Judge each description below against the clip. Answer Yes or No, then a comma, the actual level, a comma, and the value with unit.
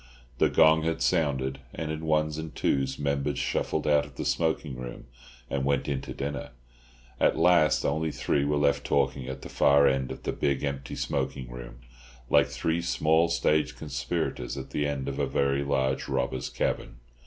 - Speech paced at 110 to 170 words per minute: No, average, 180 wpm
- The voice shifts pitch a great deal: No, narrow, 2.6 semitones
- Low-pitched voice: Yes, very low, 70 Hz